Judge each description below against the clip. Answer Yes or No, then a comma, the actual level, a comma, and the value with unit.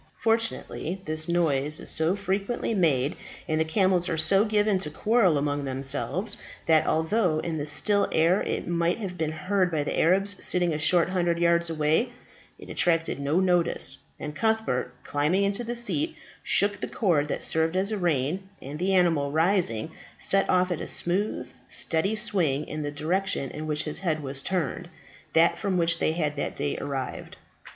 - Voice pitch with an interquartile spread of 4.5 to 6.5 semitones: No, average, 4.1 semitones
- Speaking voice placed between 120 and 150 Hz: No, medium, 170 Hz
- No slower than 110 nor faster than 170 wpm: No, average, 180 wpm